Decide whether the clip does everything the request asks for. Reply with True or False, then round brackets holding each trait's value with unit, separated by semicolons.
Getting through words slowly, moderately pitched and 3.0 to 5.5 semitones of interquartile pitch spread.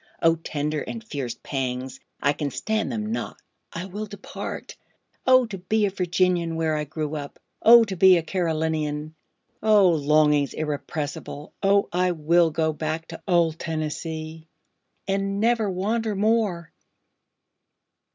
True (125 wpm; 165 Hz; 4.4 semitones)